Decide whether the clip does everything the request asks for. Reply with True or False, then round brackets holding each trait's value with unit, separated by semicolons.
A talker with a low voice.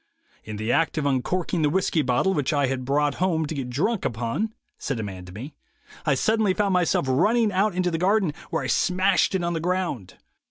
False (160 Hz)